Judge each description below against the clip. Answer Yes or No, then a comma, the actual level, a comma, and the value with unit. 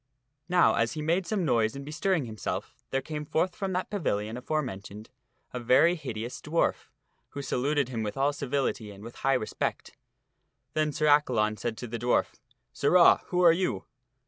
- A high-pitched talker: No, low, 135 Hz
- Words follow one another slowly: No, average, 175 wpm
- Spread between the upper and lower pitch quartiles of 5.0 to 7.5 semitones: Yes, wide, 5.4 semitones